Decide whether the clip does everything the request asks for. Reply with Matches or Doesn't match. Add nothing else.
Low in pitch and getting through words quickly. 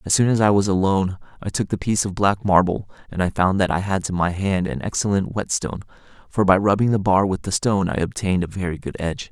Matches